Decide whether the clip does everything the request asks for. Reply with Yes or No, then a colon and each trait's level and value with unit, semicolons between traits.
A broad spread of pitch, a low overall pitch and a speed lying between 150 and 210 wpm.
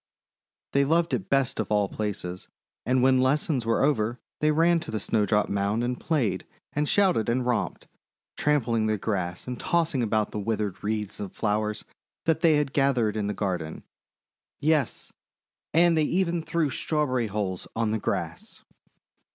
Yes: wide, 6.0 semitones; low, 120 Hz; average, 160 wpm